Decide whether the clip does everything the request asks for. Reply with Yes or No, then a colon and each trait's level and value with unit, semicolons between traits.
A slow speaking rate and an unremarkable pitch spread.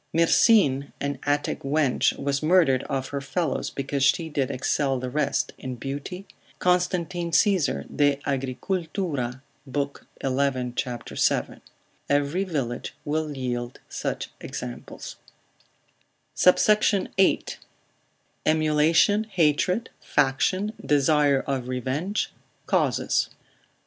Yes: slow, 95 wpm; average, 4.4 semitones